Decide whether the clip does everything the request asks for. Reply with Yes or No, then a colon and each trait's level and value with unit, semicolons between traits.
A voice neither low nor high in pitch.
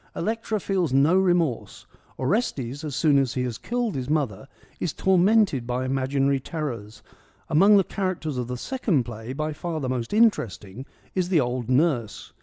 Yes: medium, 145 Hz